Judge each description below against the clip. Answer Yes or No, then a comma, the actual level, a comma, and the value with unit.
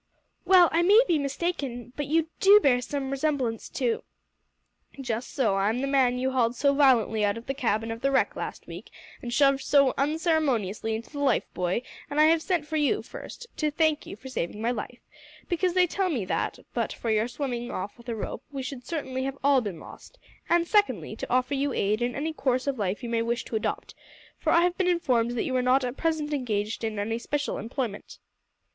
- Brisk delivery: Yes, fast, 220 wpm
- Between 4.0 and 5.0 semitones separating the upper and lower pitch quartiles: Yes, average, 4.5 semitones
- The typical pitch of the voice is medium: No, very high, 265 Hz